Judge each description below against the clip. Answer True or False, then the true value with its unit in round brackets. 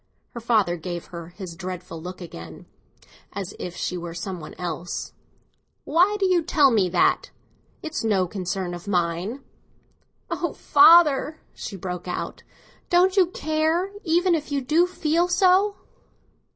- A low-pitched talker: False (210 Hz)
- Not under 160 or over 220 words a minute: False (145 wpm)